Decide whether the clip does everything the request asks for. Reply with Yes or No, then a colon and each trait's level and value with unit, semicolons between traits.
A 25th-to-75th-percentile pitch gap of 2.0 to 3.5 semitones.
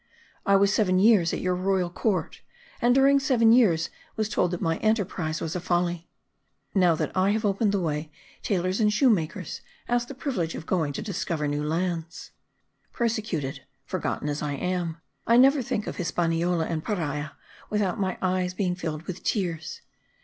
No: average, 4.2 semitones